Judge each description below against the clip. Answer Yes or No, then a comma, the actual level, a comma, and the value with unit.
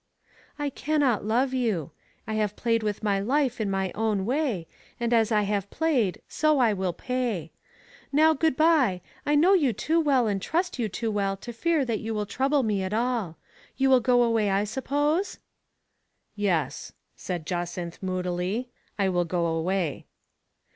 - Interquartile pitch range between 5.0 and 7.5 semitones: Yes, wide, 5.5 semitones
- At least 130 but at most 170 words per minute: No, average, 180 wpm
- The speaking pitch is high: Yes, high, 220 Hz